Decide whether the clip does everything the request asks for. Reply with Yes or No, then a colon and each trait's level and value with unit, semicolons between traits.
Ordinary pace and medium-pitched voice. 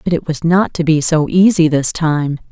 No: fast, 240 wpm; medium, 160 Hz